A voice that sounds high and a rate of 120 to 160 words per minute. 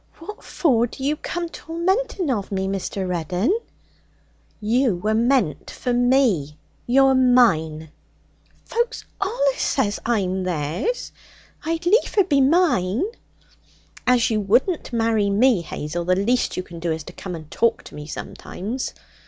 Yes: high, 230 Hz; average, 140 wpm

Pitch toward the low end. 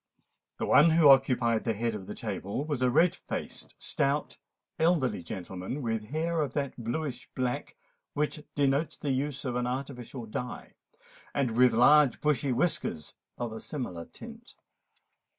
Yes: low, 130 Hz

